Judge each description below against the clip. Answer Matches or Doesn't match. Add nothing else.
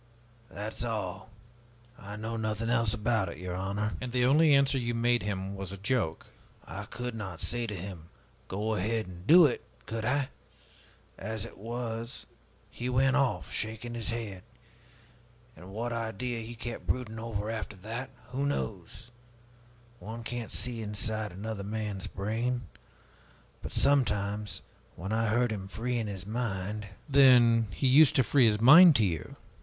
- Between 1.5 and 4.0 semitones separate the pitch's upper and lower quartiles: Matches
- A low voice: Matches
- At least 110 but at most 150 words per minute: Doesn't match